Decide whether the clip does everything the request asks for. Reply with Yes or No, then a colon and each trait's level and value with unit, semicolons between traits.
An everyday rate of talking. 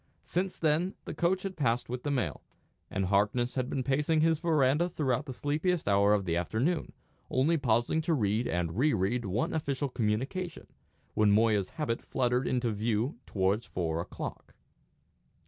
Yes: average, 165 wpm